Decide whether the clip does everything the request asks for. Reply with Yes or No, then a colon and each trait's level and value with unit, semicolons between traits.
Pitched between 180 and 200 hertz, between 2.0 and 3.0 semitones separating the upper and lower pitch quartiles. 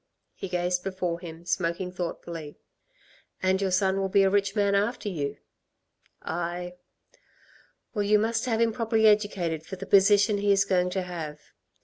Yes: high, 190 Hz; narrow, 2.6 semitones